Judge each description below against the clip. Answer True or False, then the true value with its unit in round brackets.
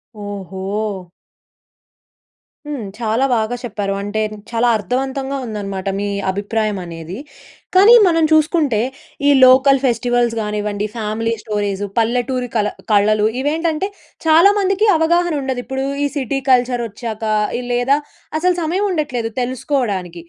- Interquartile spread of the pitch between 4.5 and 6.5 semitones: True (5.0 semitones)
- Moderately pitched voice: False (245 Hz)